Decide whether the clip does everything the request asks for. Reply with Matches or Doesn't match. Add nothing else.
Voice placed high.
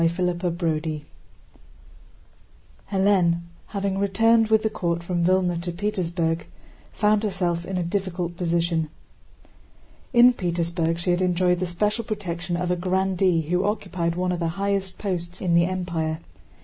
Doesn't match